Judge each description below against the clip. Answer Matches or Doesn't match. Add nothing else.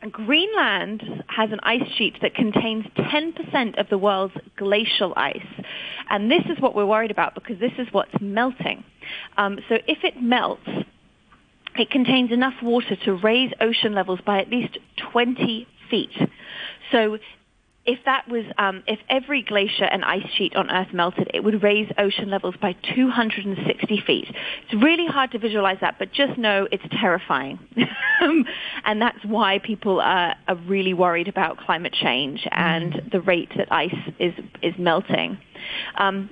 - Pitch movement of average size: Matches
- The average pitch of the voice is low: Doesn't match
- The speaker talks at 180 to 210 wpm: Doesn't match